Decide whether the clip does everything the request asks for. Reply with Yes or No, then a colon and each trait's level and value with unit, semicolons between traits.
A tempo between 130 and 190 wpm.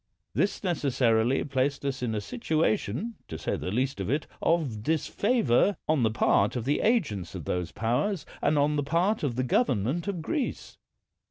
Yes: average, 175 wpm